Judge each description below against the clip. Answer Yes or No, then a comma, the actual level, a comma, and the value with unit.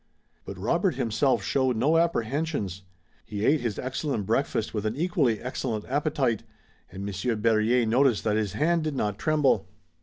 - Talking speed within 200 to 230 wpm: No, average, 155 wpm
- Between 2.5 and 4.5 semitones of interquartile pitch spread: No, average, 5.1 semitones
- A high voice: No, low, 120 Hz